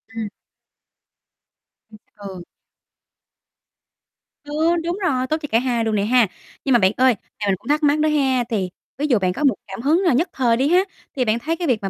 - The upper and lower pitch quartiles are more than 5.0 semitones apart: Yes, wide, 5.4 semitones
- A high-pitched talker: Yes, very high, 255 Hz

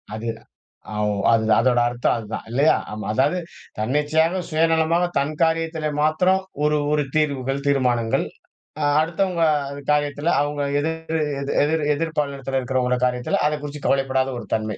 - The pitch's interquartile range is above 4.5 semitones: No, average, 3.8 semitones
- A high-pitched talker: No, medium, 145 Hz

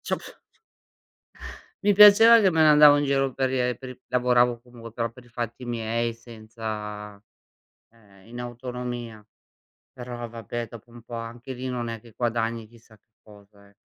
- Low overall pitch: Yes, low, 120 Hz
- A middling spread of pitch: No, narrow, 1.8 semitones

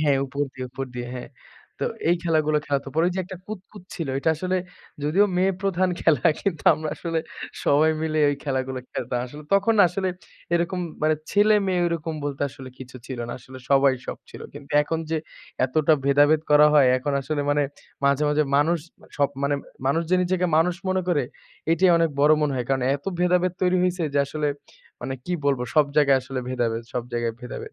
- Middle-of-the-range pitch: Yes, medium, 150 Hz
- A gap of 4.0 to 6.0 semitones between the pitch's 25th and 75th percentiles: Yes, average, 4.4 semitones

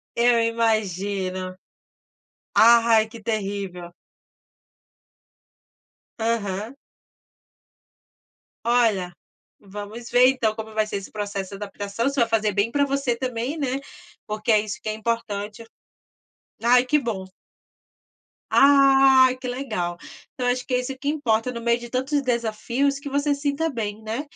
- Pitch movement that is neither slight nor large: Yes, average, 3.6 semitones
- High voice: Yes, high, 230 Hz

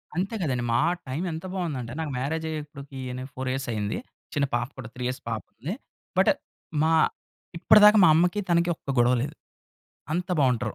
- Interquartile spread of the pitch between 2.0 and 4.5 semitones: No, average, 5.0 semitones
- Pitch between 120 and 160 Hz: Yes, medium, 140 Hz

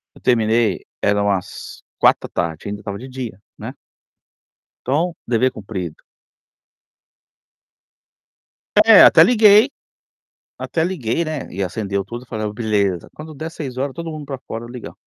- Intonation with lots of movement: Yes, wide, 7.0 semitones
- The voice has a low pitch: Yes, low, 120 Hz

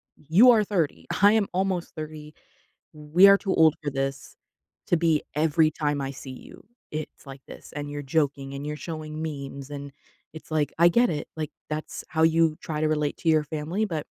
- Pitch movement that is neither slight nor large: No, narrow, 2.2 semitones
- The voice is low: No, medium, 155 Hz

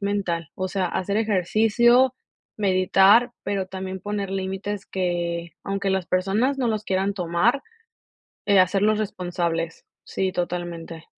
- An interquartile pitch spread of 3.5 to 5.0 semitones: No, narrow, 2.6 semitones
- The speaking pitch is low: No, high, 190 Hz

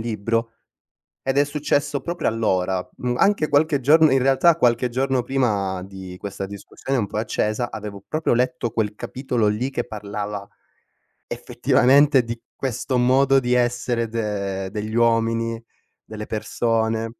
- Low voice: Yes, low, 115 Hz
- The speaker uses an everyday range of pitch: Yes, average, 3.8 semitones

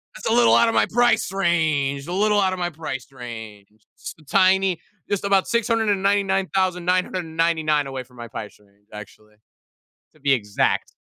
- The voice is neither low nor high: Yes, medium, 170 Hz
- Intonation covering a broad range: Yes, wide, 6.8 semitones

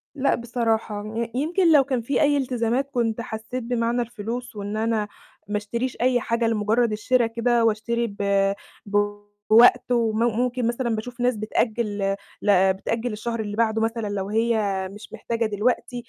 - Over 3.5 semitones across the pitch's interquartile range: No, narrow, 2.4 semitones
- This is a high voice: Yes, high, 230 Hz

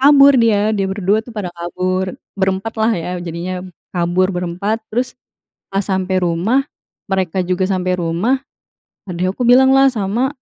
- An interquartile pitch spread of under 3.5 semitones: No, average, 3.8 semitones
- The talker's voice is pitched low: No, high, 190 Hz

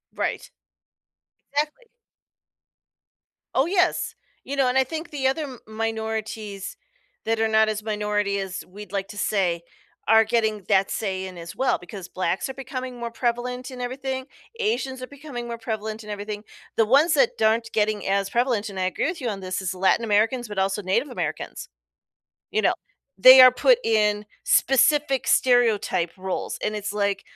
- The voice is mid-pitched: No, high, 220 Hz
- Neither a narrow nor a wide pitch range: Yes, average, 4.2 semitones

